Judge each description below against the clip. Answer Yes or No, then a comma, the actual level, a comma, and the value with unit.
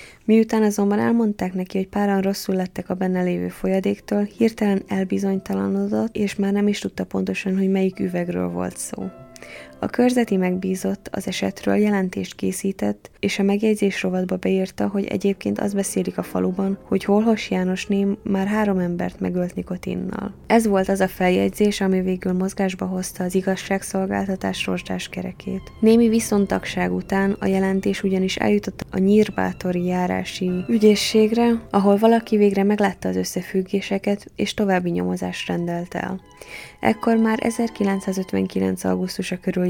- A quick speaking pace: No, average, 140 wpm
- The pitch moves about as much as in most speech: No, narrow, 2.3 semitones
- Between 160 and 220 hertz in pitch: Yes, high, 190 Hz